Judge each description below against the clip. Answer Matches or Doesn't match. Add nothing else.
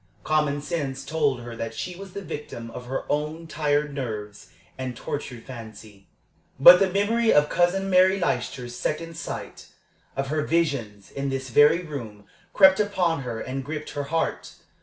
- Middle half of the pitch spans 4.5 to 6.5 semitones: Matches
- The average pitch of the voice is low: Doesn't match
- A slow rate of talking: Doesn't match